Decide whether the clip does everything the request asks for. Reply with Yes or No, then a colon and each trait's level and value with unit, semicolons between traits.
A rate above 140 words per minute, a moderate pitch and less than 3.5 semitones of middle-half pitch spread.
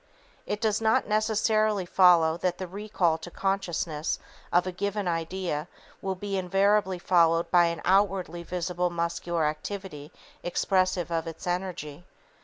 No: slow, 135 wpm; medium, 180 Hz; narrow, 2.6 semitones